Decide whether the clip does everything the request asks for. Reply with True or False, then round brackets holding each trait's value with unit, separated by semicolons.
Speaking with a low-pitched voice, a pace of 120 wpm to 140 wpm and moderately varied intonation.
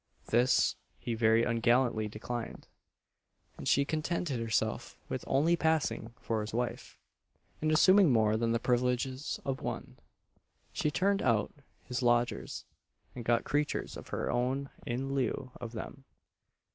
True (125 Hz; 135 wpm; 3.3 semitones)